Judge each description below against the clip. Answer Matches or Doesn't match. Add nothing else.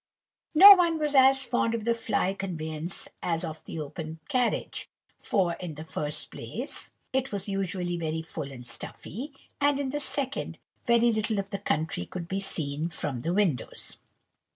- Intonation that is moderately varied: Doesn't match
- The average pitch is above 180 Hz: Matches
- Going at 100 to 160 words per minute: Doesn't match